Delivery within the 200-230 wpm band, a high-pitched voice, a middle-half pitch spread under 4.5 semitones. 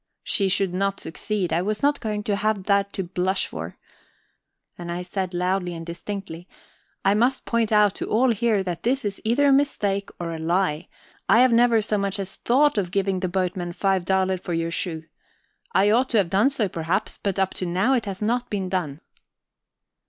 Yes: fast, 205 wpm; high, 195 Hz; average, 3.2 semitones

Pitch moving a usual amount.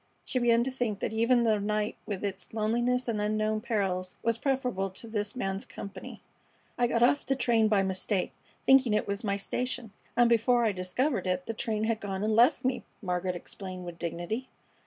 Yes: average, 3.6 semitones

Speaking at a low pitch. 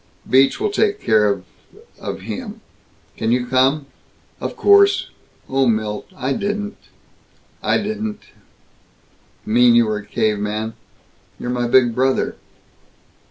Yes: low, 130 Hz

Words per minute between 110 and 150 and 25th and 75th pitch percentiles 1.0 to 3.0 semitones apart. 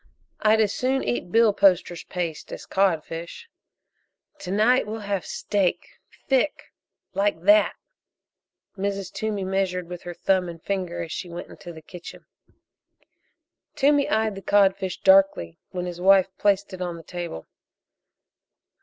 Yes: average, 140 wpm; average, 2.7 semitones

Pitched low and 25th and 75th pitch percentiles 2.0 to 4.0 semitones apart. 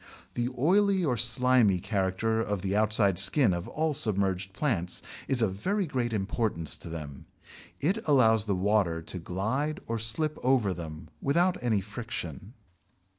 No: low, 110 Hz; average, 5.3 semitones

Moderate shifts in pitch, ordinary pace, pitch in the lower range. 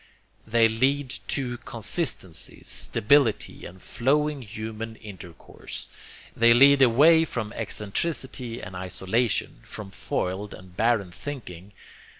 No: average, 5.0 semitones; slow, 105 wpm; low, 115 Hz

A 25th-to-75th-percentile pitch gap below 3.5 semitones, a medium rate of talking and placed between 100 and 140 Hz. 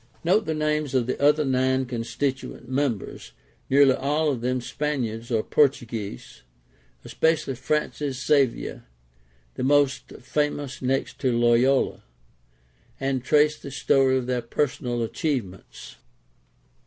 No: average, 2.9 semitones; slow, 115 wpm; low, 135 Hz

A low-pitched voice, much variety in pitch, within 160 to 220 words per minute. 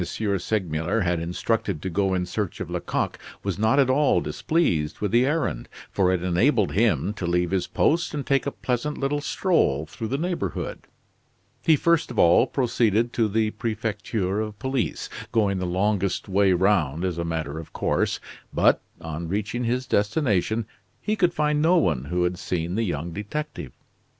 Yes: low, 105 Hz; wide, 6.0 semitones; average, 175 wpm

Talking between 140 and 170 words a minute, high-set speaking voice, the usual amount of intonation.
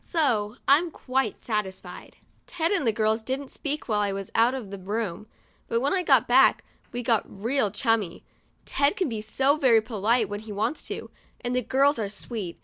No: average, 200 wpm; high, 230 Hz; average, 4.5 semitones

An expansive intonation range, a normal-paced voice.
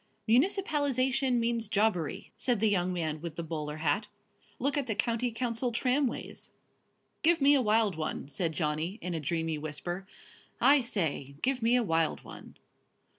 Yes: wide, 7.4 semitones; average, 160 wpm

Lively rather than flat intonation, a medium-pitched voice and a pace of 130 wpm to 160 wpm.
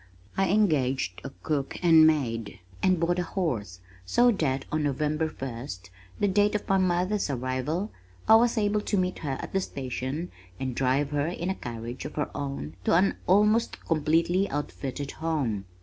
No: wide, 6.0 semitones; medium, 155 Hz; average, 170 wpm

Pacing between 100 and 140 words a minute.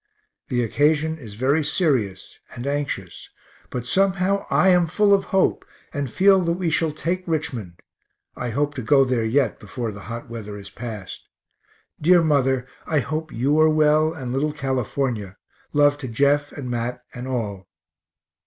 No: average, 160 wpm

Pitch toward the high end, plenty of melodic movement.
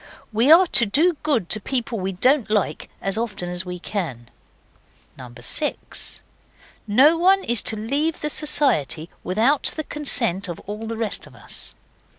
Yes: high, 225 Hz; wide, 7.2 semitones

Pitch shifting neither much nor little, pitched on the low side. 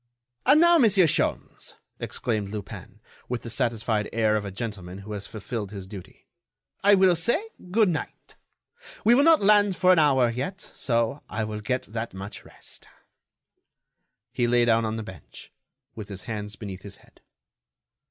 No: wide, 9.0 semitones; low, 115 Hz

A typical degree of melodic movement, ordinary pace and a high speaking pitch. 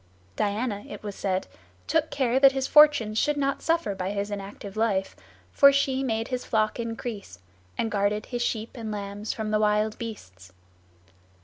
Yes: average, 4.1 semitones; average, 170 wpm; high, 220 Hz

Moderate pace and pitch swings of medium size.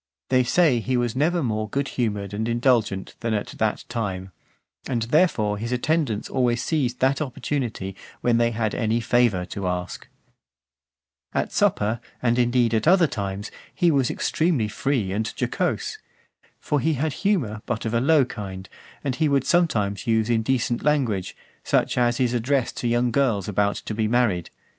Yes: average, 170 wpm; average, 3.8 semitones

